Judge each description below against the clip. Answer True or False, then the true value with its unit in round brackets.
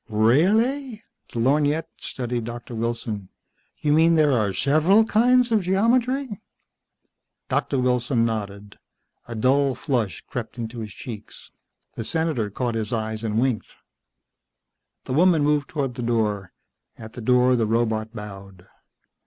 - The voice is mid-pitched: False (125 Hz)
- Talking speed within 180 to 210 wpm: False (135 wpm)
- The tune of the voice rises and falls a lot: True (5.9 semitones)